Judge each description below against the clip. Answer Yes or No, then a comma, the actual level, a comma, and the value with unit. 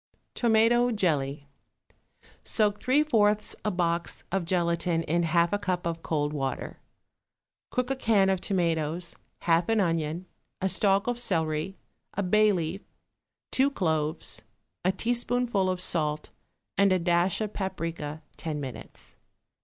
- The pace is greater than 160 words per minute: No, slow, 135 wpm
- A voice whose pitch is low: No, medium, 180 Hz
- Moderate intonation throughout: Yes, average, 4.2 semitones